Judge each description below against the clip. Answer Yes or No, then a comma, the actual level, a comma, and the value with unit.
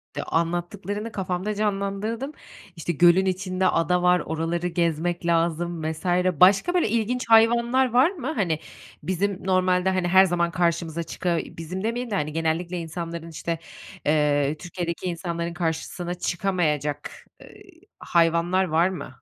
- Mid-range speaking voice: Yes, medium, 175 Hz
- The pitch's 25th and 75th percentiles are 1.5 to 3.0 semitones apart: Yes, average, 2.7 semitones